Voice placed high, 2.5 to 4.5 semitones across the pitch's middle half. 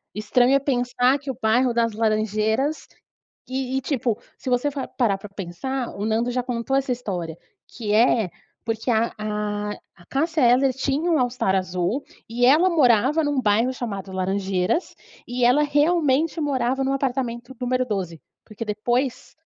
Yes: high, 245 Hz; average, 4.0 semitones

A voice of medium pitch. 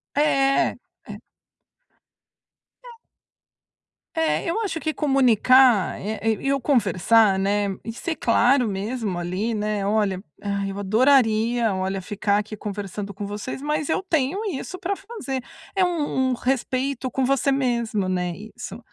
No: high, 235 Hz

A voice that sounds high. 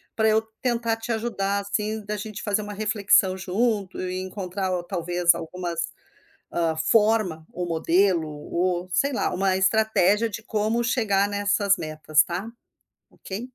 Yes: high, 200 Hz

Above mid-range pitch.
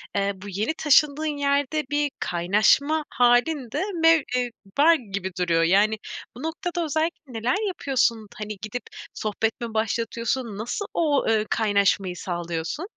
Yes: high, 235 Hz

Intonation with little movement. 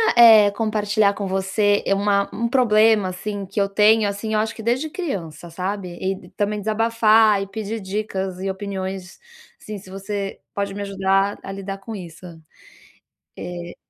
Yes: narrow, 2.0 semitones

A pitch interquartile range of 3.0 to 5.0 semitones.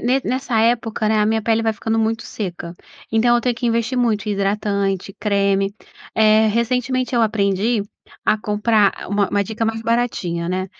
No: narrow, 2.5 semitones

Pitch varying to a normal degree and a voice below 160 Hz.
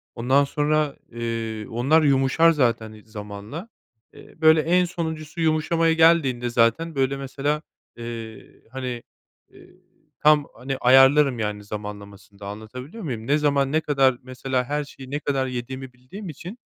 Yes: average, 4.5 semitones; low, 135 Hz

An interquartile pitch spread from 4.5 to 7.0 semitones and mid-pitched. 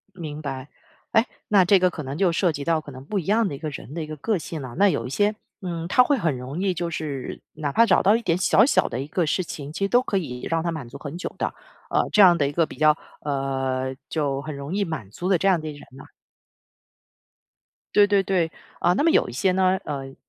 Yes: average, 5.2 semitones; medium, 165 Hz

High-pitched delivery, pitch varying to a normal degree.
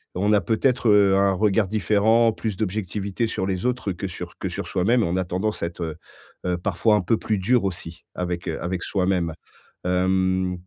No: very low, 95 Hz; average, 3.0 semitones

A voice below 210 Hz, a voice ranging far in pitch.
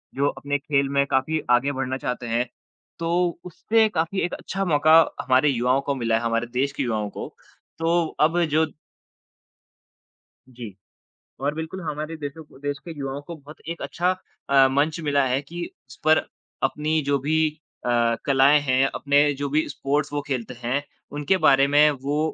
No: medium, 140 Hz; average, 2.9 semitones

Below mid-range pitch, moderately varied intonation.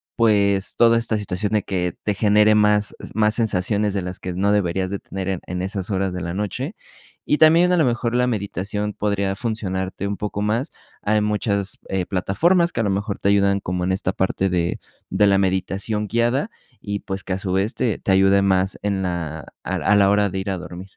No: low, 100 Hz; narrow, 2.0 semitones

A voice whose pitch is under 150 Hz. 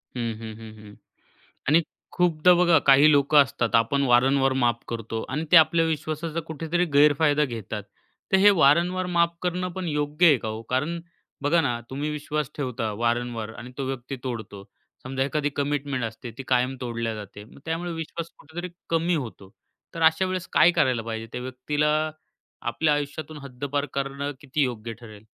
Yes: medium, 140 Hz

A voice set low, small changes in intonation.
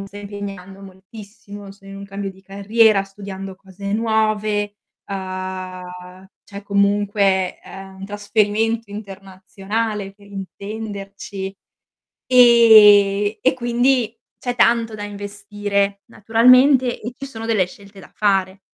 No: high, 205 Hz; narrow, 2.0 semitones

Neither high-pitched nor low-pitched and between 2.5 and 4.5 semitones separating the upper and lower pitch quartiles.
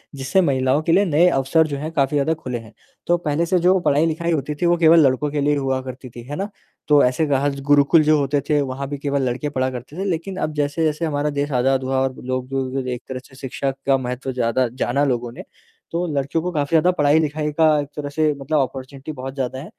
Yes: medium, 145 Hz; average, 2.9 semitones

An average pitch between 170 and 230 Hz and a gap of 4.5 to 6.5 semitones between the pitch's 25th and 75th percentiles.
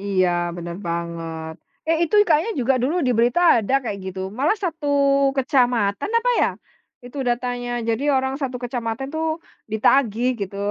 No: high, 245 Hz; average, 5.3 semitones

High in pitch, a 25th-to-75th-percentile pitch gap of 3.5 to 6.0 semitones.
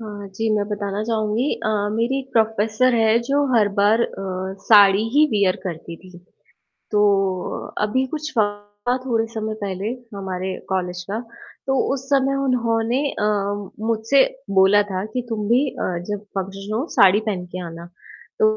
No: high, 215 Hz; average, 3.0 semitones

